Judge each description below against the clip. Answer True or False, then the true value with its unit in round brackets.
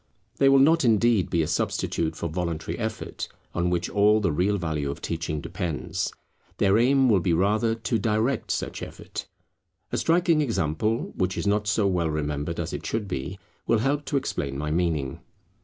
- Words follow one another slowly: False (180 wpm)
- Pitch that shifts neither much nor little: False (5.9 semitones)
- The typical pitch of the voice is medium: False (100 Hz)